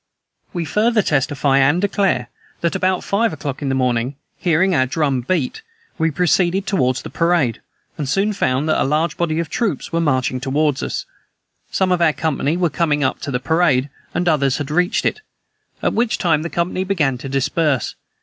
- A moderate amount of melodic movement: Yes, average, 4.6 semitones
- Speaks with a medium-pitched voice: Yes, medium, 155 Hz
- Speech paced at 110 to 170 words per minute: No, average, 190 wpm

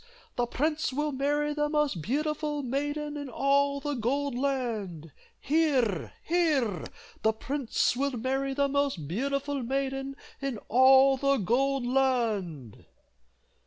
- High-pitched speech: Yes, very high, 275 Hz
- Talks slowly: Yes, slow, 125 wpm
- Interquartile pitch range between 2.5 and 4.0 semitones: Yes, average, 2.9 semitones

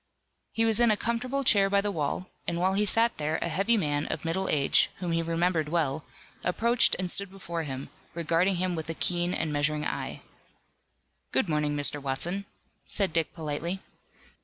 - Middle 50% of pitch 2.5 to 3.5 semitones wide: No, average, 4.2 semitones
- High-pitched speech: No, medium, 175 Hz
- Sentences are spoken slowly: No, average, 185 wpm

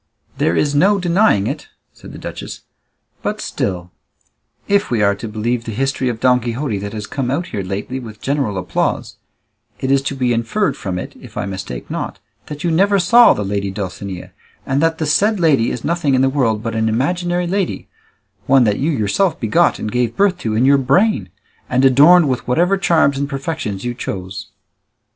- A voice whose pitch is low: Yes, low, 130 Hz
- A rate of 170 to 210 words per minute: Yes, average, 195 wpm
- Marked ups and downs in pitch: Yes, wide, 7.3 semitones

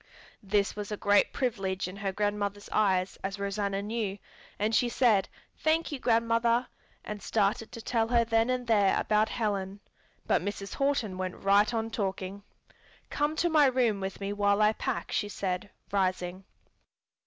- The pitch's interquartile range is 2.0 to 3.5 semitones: Yes, average, 2.7 semitones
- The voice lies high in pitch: Yes, high, 205 Hz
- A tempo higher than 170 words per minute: No, average, 165 wpm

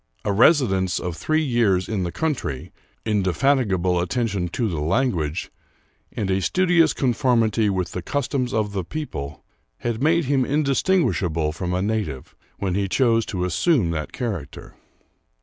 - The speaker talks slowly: No, average, 150 wpm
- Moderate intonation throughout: No, wide, 6.6 semitones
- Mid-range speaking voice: No, low, 105 Hz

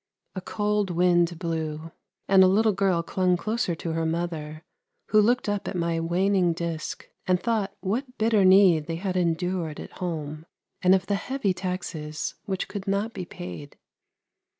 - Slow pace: No, average, 165 wpm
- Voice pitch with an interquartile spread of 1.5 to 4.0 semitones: Yes, average, 3.2 semitones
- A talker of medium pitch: Yes, medium, 180 Hz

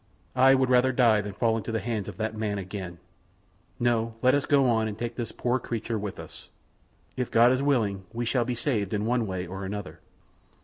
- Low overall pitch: Yes, low, 115 Hz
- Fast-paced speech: Yes, fast, 220 wpm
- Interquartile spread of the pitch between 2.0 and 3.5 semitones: Yes, average, 3.2 semitones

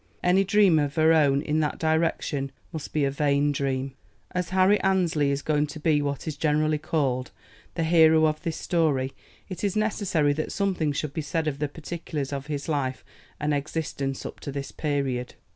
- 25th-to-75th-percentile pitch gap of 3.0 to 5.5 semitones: No, narrow, 2.5 semitones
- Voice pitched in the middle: Yes, medium, 150 Hz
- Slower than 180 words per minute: No, average, 190 wpm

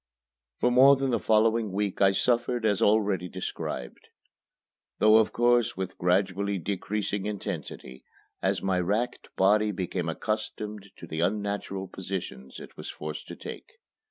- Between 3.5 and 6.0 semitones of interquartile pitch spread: No, average, 2.7 semitones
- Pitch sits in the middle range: No, low, 100 Hz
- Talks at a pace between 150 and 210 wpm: No, average, 140 wpm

